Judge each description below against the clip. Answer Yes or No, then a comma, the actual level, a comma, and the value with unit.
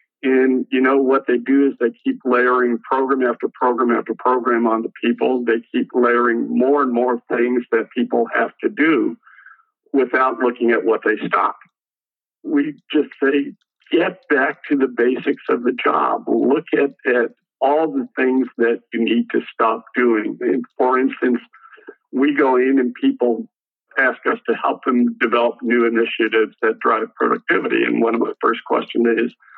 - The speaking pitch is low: Yes, low, 125 Hz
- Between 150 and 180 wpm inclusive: Yes, average, 170 wpm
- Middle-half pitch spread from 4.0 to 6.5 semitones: No, average, 2.9 semitones